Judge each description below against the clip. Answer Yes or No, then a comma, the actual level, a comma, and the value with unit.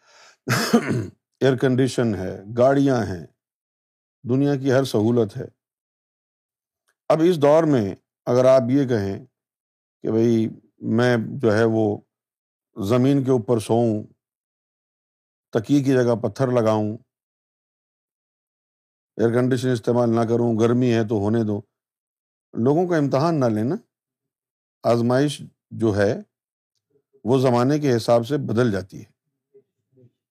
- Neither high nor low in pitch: No, low, 120 Hz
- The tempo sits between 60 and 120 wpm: Yes, average, 115 wpm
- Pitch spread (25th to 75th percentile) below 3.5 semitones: Yes, average, 3.1 semitones